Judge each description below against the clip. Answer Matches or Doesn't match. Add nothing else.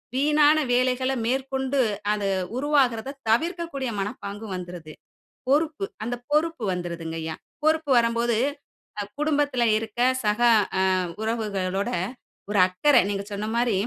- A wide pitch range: Matches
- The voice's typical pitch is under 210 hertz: Doesn't match